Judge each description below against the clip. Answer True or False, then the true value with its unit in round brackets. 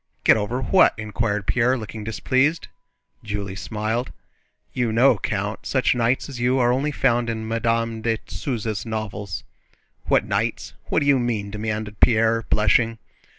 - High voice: False (115 Hz)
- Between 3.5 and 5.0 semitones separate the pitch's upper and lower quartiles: False (2.4 semitones)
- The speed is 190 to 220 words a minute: False (150 wpm)